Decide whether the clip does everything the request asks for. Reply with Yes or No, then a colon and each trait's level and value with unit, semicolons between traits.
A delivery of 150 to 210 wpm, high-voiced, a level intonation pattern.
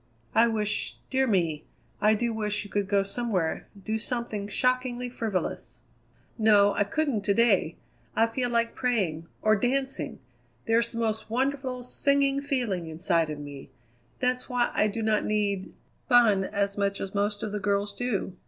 No: average, 160 wpm; high, 215 Hz; average, 3.4 semitones